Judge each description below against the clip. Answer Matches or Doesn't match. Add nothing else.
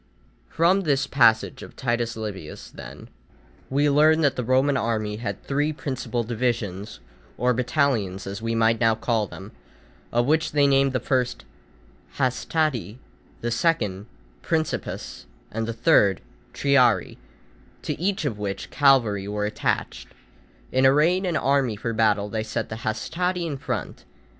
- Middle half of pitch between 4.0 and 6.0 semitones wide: Matches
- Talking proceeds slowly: Doesn't match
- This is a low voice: Matches